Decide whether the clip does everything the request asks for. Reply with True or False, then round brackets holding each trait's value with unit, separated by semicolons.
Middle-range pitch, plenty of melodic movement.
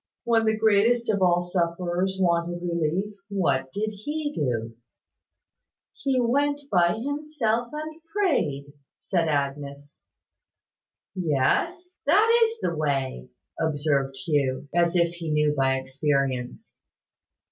True (175 Hz; 8.4 semitones)